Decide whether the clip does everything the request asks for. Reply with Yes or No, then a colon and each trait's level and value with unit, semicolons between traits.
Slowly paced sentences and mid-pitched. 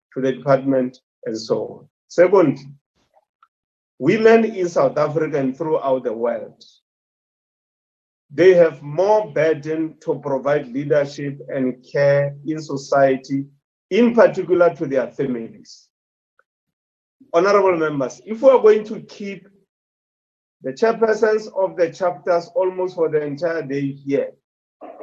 Yes: slow, 120 wpm; medium, 155 Hz